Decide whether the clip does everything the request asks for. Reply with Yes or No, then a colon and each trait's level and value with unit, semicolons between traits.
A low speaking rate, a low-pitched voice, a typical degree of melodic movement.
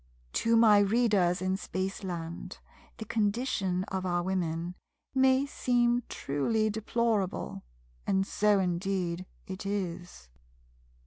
No: slow, 105 wpm; high, 195 Hz; average, 3.7 semitones